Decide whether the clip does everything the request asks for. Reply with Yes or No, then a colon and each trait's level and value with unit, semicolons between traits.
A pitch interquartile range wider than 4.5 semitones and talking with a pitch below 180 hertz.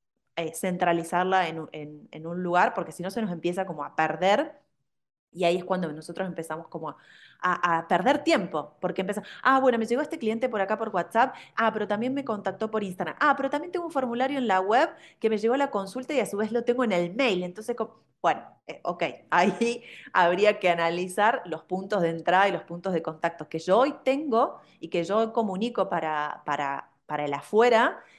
No: wide, 5.5 semitones; high, 190 Hz